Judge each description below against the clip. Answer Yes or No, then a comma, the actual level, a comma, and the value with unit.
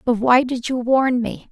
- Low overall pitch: No, high, 245 Hz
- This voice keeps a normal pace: No, fast, 235 wpm